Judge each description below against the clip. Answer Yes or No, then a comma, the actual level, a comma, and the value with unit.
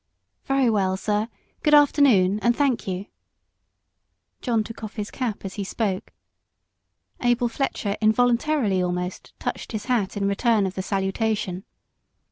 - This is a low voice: No, high, 215 Hz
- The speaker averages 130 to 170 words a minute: Yes, slow, 135 wpm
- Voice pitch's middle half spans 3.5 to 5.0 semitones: Yes, average, 3.9 semitones